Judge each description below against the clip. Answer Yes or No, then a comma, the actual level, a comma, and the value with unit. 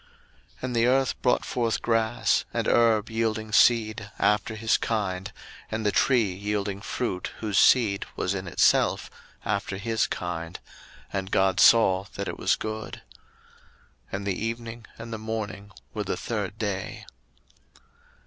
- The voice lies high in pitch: No, low, 110 Hz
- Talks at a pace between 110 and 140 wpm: No, average, 150 wpm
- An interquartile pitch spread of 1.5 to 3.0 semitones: Yes, narrow, 2.5 semitones